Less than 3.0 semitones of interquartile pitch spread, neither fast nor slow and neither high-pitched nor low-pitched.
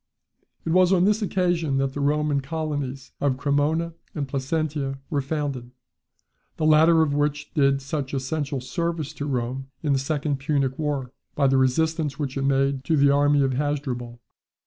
Yes: narrow, 2.4 semitones; average, 170 wpm; medium, 145 Hz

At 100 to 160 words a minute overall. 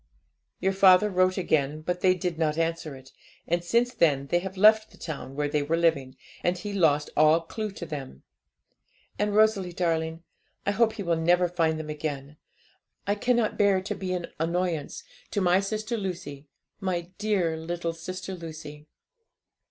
No: average, 170 wpm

